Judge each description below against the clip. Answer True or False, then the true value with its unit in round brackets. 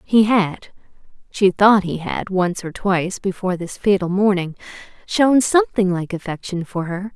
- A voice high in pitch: True (195 Hz)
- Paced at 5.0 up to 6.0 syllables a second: False (4.7 syllables/s)